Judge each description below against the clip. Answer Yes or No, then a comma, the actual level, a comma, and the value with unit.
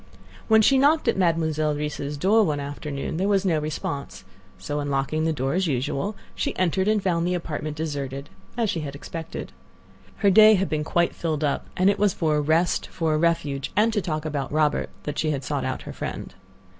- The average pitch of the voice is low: No, medium, 155 Hz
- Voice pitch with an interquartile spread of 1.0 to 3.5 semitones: No, average, 4.3 semitones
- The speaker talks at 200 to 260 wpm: Yes, fast, 205 wpm